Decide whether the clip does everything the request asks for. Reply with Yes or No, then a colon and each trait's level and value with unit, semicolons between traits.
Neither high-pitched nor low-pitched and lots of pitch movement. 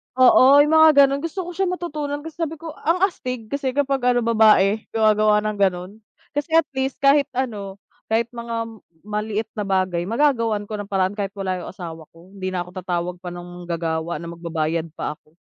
No: high, 215 Hz; wide, 7.0 semitones